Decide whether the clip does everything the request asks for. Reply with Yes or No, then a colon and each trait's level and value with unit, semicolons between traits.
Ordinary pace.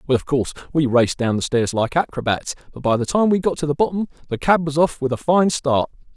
No: fast, 265 wpm